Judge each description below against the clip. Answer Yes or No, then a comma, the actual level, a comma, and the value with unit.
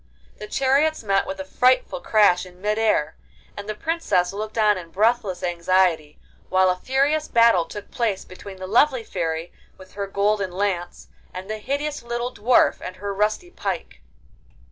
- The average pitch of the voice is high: Yes, high, 205 Hz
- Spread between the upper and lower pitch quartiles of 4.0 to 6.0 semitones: Yes, average, 4.3 semitones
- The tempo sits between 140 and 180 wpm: Yes, average, 165 wpm